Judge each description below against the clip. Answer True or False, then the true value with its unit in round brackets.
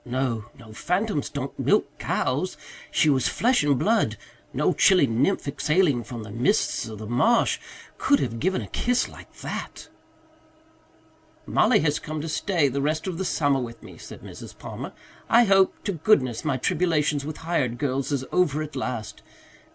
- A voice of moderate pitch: True (145 Hz)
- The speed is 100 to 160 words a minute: False (170 wpm)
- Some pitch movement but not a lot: False (6.0 semitones)